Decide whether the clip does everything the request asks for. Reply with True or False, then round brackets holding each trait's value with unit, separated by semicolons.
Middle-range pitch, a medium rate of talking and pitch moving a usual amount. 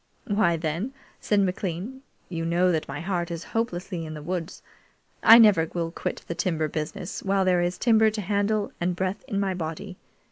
True (180 Hz; 185 wpm; 3.3 semitones)